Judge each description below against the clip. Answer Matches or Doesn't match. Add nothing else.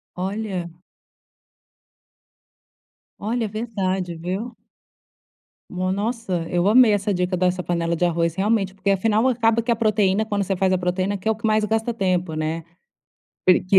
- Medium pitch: Doesn't match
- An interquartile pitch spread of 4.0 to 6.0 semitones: Doesn't match